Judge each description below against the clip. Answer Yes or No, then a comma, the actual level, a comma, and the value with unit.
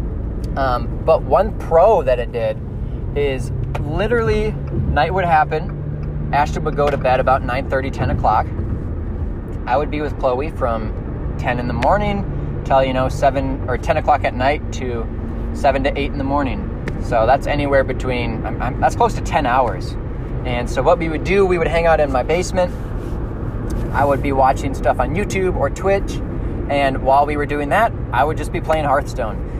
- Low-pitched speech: Yes, low, 125 Hz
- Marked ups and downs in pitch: No, average, 4.1 semitones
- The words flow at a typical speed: Yes, average, 185 wpm